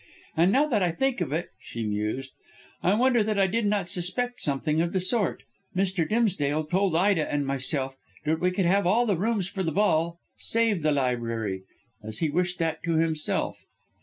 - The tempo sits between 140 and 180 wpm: No, average, 190 wpm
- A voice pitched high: No, medium, 175 Hz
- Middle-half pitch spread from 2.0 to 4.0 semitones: No, average, 5.1 semitones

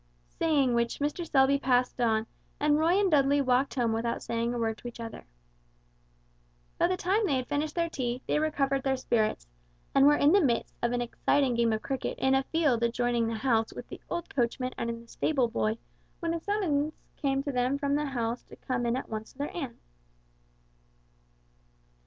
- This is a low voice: No, very high, 265 Hz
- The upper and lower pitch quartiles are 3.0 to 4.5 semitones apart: Yes, average, 3.8 semitones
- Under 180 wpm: No, average, 200 wpm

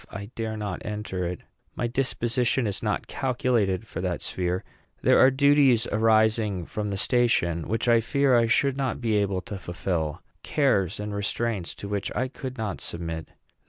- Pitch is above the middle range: No, low, 110 Hz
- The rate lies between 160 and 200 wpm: Yes, average, 170 wpm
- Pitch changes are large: No, average, 4.3 semitones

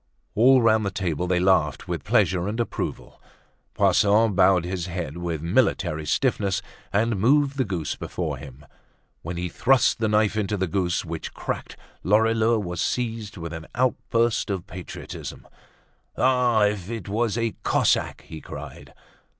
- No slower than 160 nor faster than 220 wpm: No, average, 150 wpm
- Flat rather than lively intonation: No, average, 4.5 semitones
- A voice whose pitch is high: No, low, 100 Hz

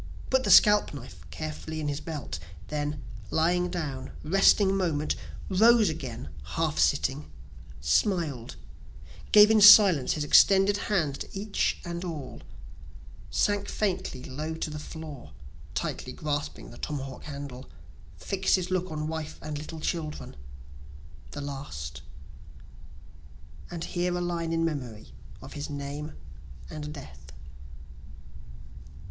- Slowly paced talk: Yes, slow, 125 wpm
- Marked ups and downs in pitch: No, average, 4.0 semitones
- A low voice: No, medium, 155 Hz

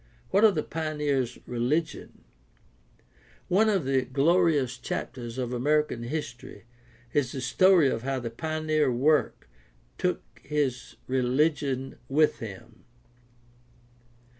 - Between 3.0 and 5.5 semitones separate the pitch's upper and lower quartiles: Yes, average, 3.7 semitones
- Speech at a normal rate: No, slow, 110 wpm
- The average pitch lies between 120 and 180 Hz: Yes, low, 135 Hz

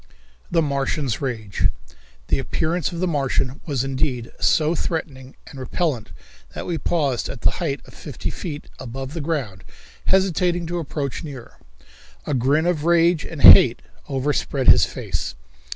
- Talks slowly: No, average, 150 wpm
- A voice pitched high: No, medium, 145 Hz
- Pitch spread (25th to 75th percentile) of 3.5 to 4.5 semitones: Yes, average, 4.1 semitones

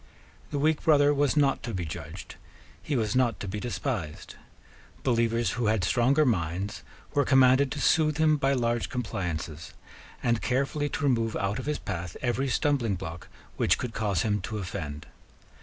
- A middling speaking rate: Yes, average, 170 wpm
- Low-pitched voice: Yes, low, 120 Hz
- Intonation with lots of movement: Yes, wide, 5.8 semitones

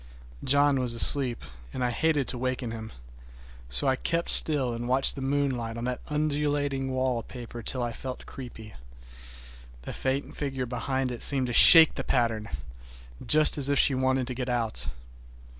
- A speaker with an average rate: Yes, average, 160 wpm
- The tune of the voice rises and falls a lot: No, narrow, 2.6 semitones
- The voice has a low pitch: Yes, low, 130 Hz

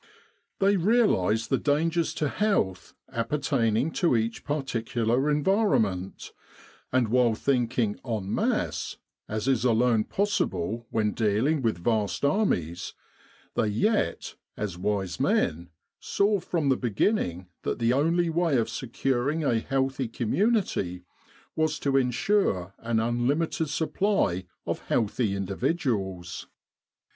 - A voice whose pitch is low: Yes, low, 120 Hz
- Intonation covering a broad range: Yes, wide, 6.4 semitones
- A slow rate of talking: Yes, slow, 115 wpm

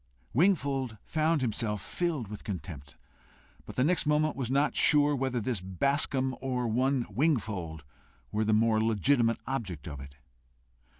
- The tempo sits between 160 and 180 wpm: No, average, 140 wpm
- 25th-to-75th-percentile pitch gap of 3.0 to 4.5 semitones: No, average, 5.0 semitones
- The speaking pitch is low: Yes, low, 125 Hz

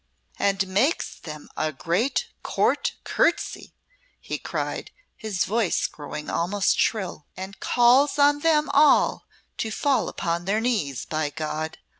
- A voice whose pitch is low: No, high, 195 Hz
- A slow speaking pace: Yes, slow, 130 wpm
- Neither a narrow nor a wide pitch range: No, wide, 7.8 semitones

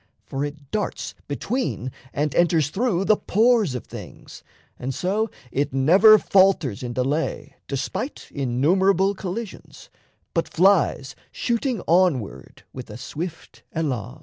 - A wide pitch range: Yes, wide, 6.6 semitones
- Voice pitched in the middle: Yes, medium, 165 Hz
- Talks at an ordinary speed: No, slow, 120 wpm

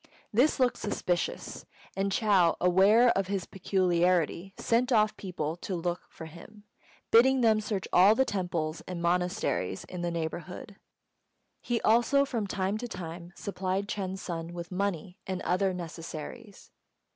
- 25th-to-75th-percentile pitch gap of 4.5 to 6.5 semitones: No, average, 3.5 semitones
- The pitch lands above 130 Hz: Yes, high, 190 Hz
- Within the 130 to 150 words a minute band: Yes, average, 145 wpm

